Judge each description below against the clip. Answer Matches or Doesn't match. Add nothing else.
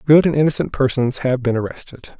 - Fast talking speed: Doesn't match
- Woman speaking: Doesn't match